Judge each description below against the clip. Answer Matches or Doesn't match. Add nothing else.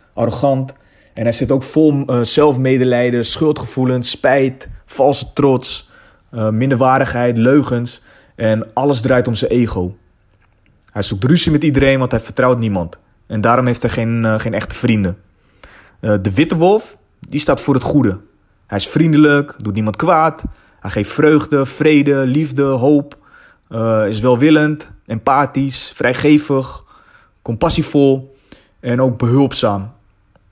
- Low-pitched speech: Matches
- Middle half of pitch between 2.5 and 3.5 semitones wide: Doesn't match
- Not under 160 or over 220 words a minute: Doesn't match